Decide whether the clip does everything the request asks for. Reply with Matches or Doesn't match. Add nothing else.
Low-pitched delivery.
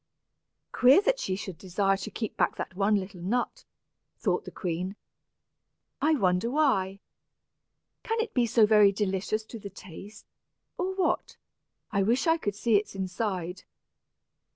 Doesn't match